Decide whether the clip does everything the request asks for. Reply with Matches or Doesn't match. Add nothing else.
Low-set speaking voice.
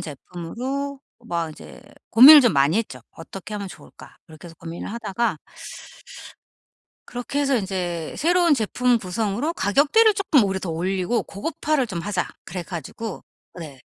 Doesn't match